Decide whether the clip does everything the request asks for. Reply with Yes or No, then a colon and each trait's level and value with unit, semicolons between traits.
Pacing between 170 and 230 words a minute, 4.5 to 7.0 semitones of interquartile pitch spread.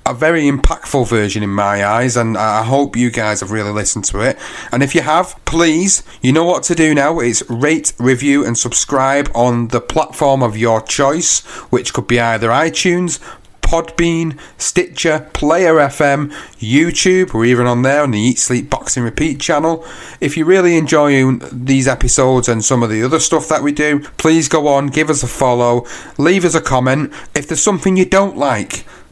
Yes: average, 190 wpm; average, 4.9 semitones